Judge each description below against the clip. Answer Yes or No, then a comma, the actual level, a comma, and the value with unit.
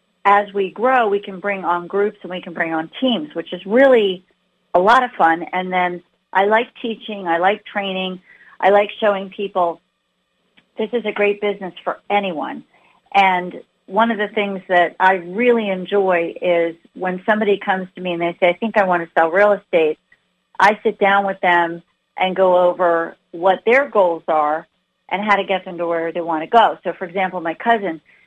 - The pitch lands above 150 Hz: Yes, high, 190 Hz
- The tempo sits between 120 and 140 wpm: No, average, 200 wpm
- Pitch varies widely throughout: No, narrow, 2.6 semitones